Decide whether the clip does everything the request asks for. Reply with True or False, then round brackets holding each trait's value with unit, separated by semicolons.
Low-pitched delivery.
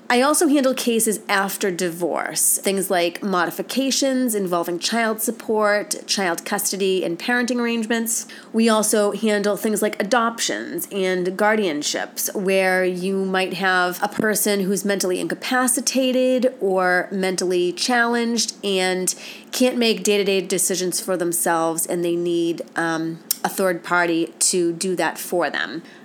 False (200 Hz)